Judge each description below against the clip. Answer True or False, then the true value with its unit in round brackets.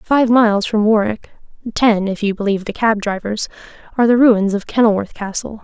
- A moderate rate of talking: True (180 wpm)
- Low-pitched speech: False (215 Hz)